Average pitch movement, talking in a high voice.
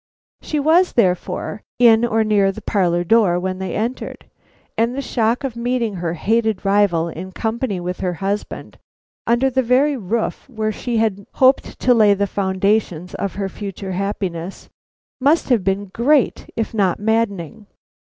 Yes: average, 3.7 semitones; high, 210 Hz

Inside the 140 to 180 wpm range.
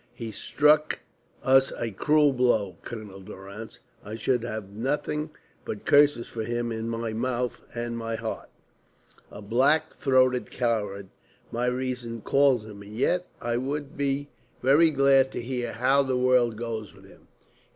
Yes: average, 150 wpm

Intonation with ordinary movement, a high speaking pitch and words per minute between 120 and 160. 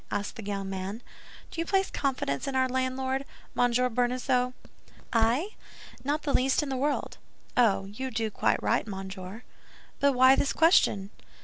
Yes: average, 4.4 semitones; very high, 250 Hz; average, 150 wpm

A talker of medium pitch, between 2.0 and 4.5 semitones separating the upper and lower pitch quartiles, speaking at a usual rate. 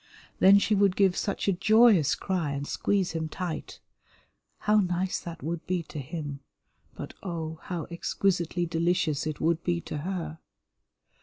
Yes: medium, 175 Hz; average, 3.1 semitones; average, 155 wpm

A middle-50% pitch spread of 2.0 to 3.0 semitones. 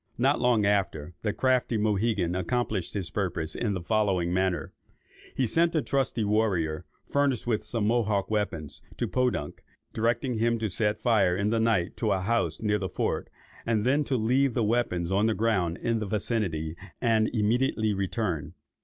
No: average, 3.8 semitones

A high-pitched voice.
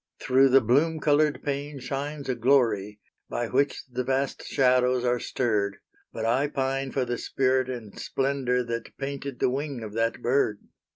No: low, 130 Hz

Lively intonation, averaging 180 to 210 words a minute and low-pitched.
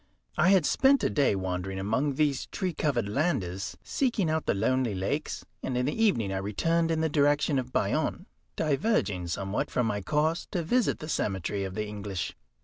Yes: wide, 8.3 semitones; average, 185 wpm; low, 130 Hz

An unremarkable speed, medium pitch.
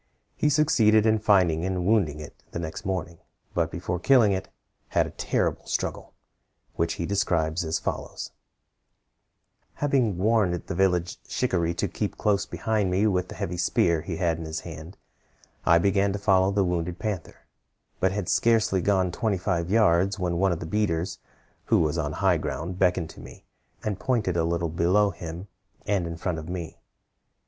No: average, 175 wpm; very low, 90 Hz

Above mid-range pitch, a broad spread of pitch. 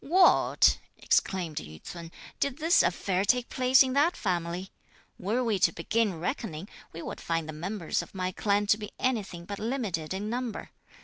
Yes: high, 200 Hz; wide, 5.8 semitones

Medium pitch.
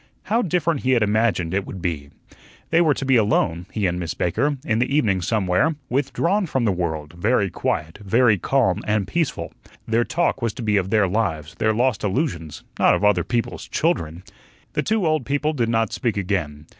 No: low, 110 Hz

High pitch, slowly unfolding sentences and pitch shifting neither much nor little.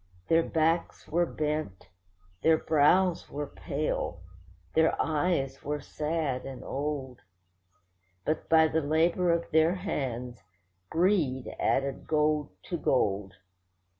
No: medium, 155 Hz; slow, 110 wpm; average, 3.3 semitones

